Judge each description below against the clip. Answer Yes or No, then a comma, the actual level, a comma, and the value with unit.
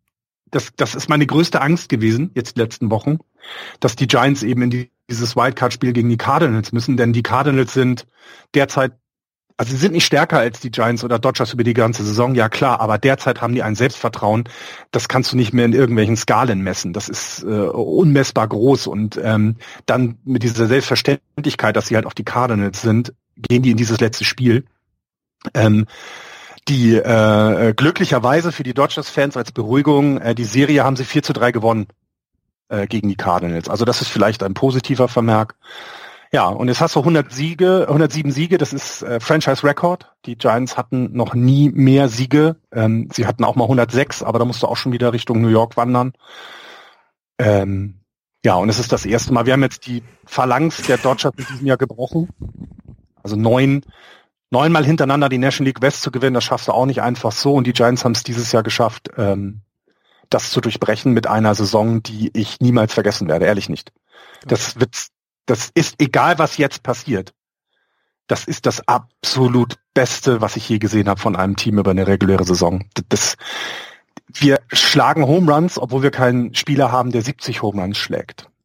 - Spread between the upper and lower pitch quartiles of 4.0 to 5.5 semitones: No, average, 3.3 semitones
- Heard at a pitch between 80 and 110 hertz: No, low, 125 Hz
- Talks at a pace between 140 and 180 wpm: No, fast, 190 wpm